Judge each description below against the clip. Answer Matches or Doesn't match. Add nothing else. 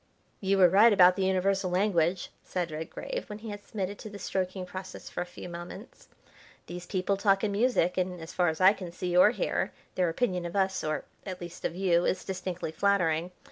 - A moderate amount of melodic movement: Doesn't match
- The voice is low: Doesn't match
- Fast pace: Matches